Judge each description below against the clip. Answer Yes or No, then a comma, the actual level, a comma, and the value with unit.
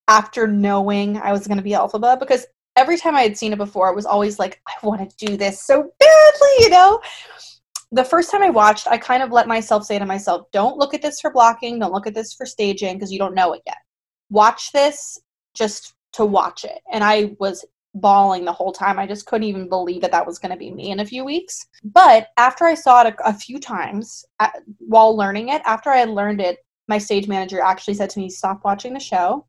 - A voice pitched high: Yes, high, 215 Hz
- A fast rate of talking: Yes, fast, 240 wpm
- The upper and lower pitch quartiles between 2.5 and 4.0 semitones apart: No, average, 4.5 semitones